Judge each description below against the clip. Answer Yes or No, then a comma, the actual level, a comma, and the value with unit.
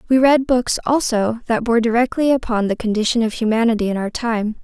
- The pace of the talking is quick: No, average, 195 wpm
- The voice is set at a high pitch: Yes, high, 230 Hz